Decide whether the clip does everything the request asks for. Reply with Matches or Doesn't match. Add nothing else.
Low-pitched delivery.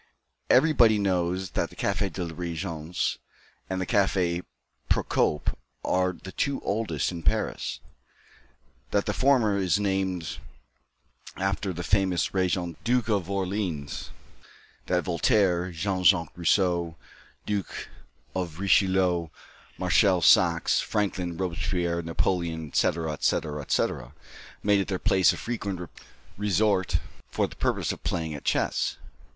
Matches